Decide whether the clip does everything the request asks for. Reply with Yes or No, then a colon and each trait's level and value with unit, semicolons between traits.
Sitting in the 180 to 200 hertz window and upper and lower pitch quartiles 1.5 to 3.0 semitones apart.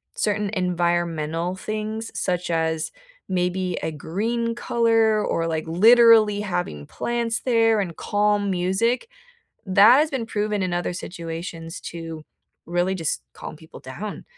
No: high, 190 Hz; average, 4.6 semitones